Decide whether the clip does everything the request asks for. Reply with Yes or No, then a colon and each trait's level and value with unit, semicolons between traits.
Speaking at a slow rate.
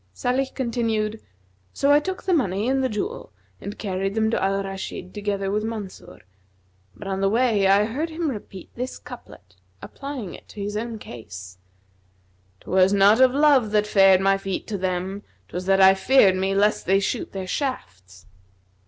No: average, 180 wpm